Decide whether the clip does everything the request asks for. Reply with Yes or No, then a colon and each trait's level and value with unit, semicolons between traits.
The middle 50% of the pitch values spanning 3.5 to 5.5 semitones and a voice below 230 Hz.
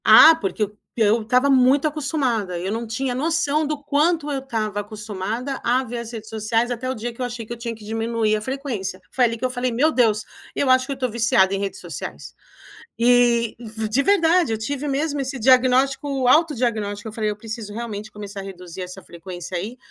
No: average, 4.0 semitones; high, 235 Hz